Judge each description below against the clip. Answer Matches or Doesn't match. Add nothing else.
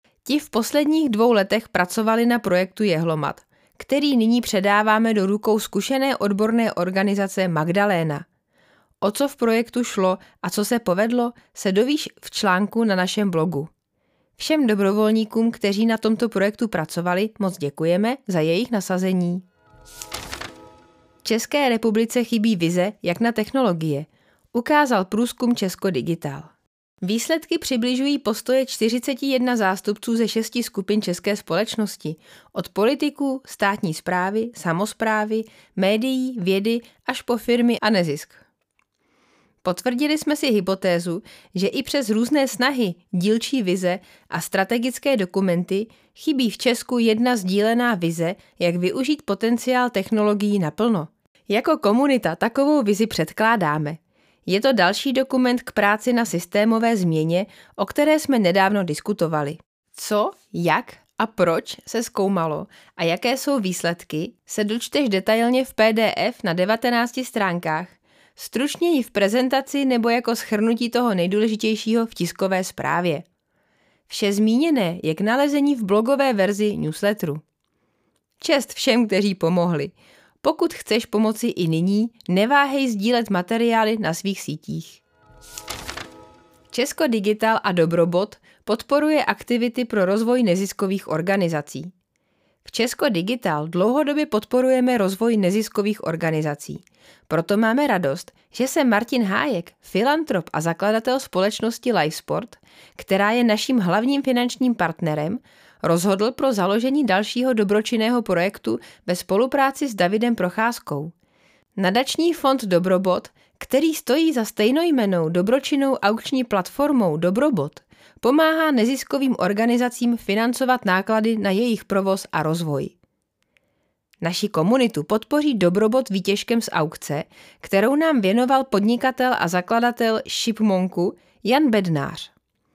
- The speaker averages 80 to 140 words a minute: Matches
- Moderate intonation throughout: Matches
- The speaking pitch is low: Doesn't match